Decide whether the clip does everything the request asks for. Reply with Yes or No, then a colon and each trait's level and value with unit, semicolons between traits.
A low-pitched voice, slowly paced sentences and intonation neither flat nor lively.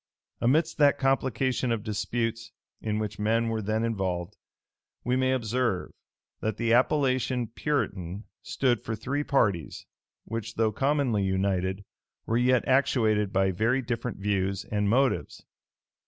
Yes: low, 115 Hz; slow, 130 wpm; average, 3.9 semitones